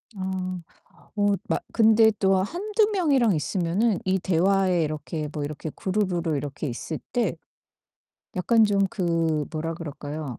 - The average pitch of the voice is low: No, medium, 185 Hz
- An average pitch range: Yes, average, 4.7 semitones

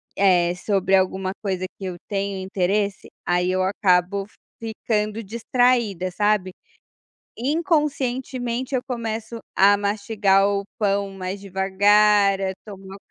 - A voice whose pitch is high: Yes, high, 200 Hz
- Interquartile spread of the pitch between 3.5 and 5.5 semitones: No, narrow, 2.5 semitones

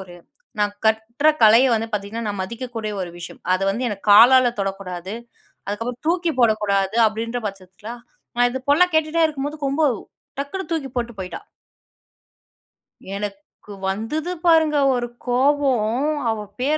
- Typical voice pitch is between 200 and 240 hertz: Yes, high, 230 Hz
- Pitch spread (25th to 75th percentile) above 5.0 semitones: Yes, wide, 5.4 semitones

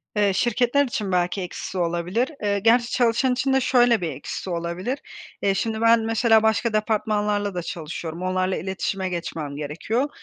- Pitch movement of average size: Yes, average, 4.5 semitones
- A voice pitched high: Yes, high, 205 Hz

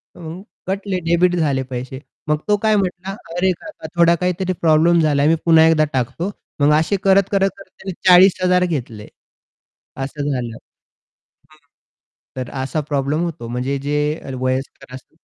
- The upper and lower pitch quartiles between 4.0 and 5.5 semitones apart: Yes, average, 4.8 semitones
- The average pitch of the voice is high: No, medium, 160 Hz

